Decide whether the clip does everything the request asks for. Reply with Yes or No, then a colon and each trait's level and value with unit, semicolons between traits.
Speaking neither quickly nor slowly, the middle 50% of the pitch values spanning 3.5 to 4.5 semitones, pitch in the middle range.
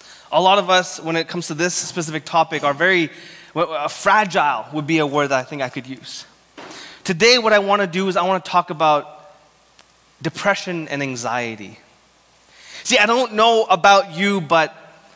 Yes: average, 185 wpm; average, 4.1 semitones; medium, 165 Hz